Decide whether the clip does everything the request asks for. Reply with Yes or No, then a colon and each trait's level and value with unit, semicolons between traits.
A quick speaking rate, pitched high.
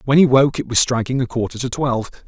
No: fast, 265 wpm; low, 125 Hz